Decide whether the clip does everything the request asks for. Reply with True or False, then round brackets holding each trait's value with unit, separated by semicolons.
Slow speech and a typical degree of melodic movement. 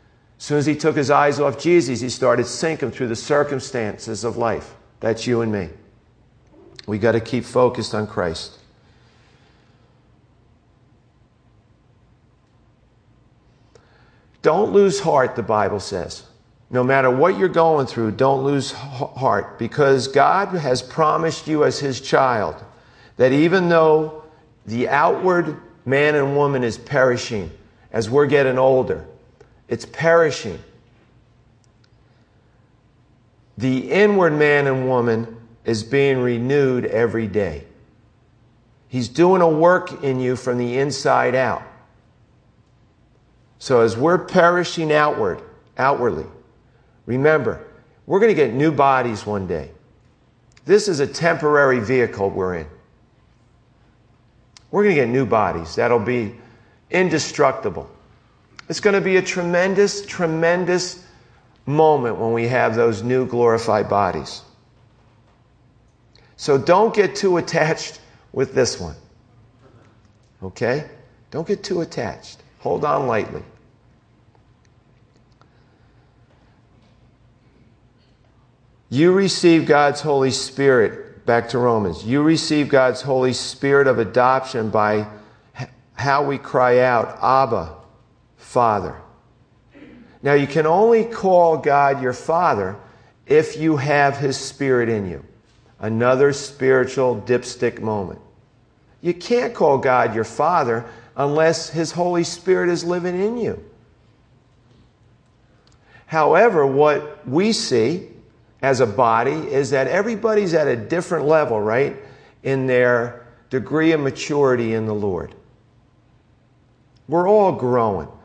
True (115 wpm; 4.3 semitones)